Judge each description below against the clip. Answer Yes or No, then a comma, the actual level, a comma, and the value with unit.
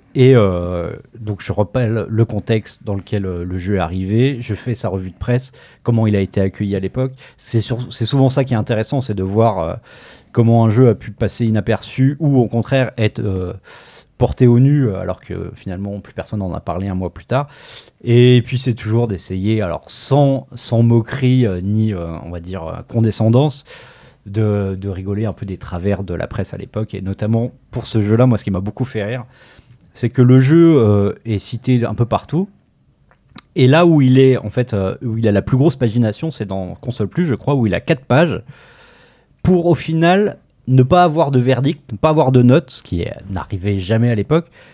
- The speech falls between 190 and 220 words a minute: Yes, average, 210 wpm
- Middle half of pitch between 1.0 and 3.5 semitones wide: No, average, 4.2 semitones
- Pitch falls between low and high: No, low, 115 Hz